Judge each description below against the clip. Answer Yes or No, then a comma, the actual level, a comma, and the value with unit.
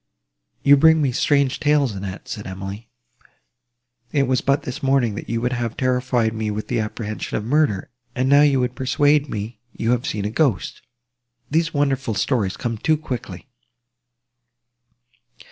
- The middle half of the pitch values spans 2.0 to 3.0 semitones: No, average, 4.3 semitones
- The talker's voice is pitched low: Yes, low, 125 Hz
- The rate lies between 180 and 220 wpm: No, average, 160 wpm